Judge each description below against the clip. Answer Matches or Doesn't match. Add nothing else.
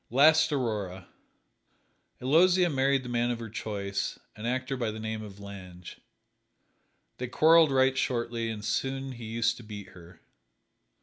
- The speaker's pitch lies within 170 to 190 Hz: Doesn't match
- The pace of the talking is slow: Doesn't match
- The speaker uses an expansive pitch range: Doesn't match